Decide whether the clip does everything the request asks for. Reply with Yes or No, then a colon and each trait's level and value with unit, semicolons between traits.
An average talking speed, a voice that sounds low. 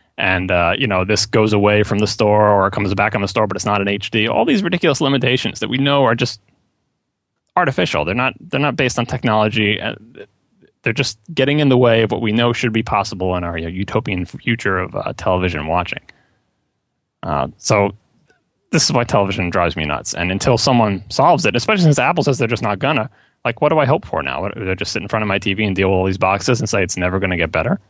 No: fast, 245 wpm; low, 105 Hz